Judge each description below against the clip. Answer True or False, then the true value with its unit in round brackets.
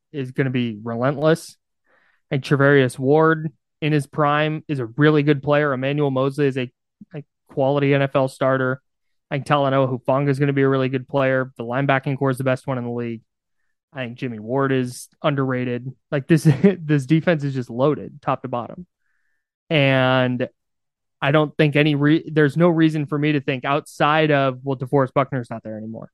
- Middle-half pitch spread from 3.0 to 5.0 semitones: False (2.4 semitones)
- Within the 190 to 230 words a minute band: True (200 wpm)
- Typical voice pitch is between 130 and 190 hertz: True (140 Hz)